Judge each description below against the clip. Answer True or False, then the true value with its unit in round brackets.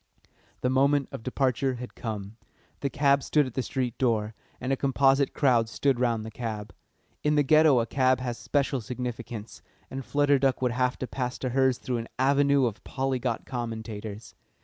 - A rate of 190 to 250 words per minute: False (180 wpm)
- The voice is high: False (130 Hz)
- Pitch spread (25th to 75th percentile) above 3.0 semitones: False (2.7 semitones)